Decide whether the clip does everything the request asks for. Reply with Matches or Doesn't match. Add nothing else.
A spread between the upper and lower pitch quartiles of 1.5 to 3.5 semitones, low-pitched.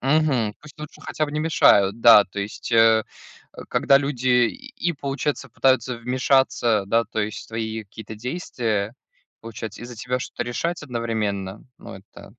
Doesn't match